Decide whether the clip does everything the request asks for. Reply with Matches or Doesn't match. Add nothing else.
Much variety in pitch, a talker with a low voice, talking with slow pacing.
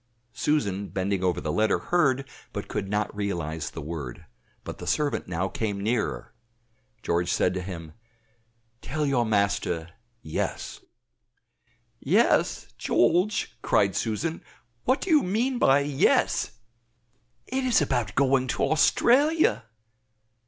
Matches